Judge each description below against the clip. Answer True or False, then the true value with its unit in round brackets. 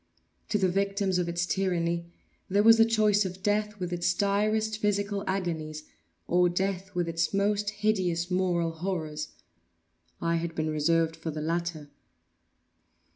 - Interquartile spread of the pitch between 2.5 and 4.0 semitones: True (3.3 semitones)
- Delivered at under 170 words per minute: True (145 wpm)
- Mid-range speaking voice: True (180 Hz)